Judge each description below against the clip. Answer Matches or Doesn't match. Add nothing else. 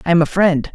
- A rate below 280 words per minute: Doesn't match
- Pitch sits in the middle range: Matches